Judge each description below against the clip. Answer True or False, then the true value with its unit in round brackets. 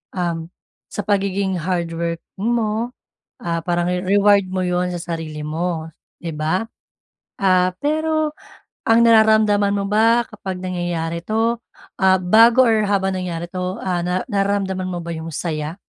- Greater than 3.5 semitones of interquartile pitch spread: False (3.2 semitones)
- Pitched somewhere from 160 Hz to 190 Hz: True (185 Hz)